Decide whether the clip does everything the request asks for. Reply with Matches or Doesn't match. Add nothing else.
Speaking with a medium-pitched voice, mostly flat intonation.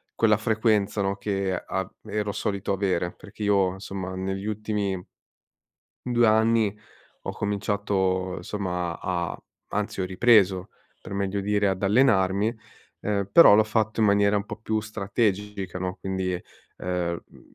Doesn't match